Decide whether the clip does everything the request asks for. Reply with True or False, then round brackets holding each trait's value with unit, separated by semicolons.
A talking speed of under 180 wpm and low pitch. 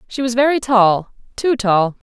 False (140 wpm; 230 Hz)